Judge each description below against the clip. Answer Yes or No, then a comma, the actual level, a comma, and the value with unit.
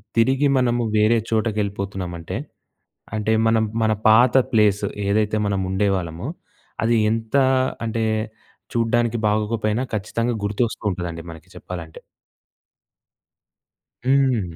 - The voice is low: Yes, low, 110 Hz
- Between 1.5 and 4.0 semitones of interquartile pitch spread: Yes, average, 2.9 semitones